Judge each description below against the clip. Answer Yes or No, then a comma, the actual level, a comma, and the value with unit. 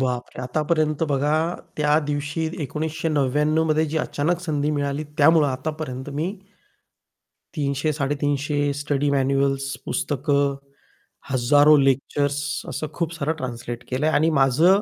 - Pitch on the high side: No, medium, 145 Hz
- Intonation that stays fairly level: Yes, narrow, 2.0 semitones